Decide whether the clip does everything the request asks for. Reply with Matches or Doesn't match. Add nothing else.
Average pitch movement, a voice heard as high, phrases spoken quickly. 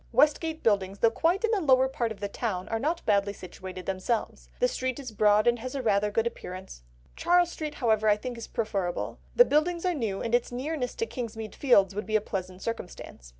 Doesn't match